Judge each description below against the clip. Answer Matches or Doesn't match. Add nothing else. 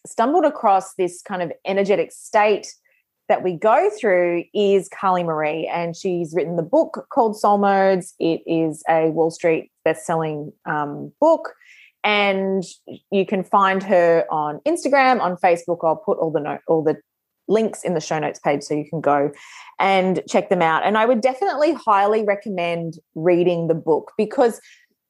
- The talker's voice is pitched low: Doesn't match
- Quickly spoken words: Doesn't match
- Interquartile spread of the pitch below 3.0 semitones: Doesn't match